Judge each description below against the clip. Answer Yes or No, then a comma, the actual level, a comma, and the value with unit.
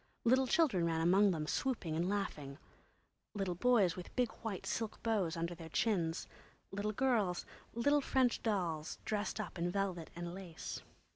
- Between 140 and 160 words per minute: Yes, average, 155 wpm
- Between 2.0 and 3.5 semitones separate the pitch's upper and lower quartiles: No, average, 4.8 semitones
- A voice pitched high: Yes, high, 195 Hz